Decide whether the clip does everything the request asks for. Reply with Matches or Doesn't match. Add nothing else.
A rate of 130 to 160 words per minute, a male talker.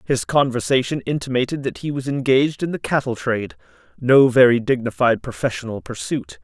Matches